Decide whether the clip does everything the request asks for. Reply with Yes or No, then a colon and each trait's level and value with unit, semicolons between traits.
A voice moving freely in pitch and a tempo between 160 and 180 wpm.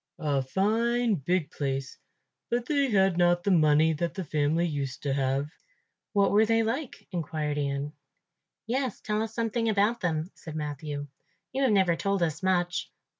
Yes: wide, 6.5 semitones; average, 165 wpm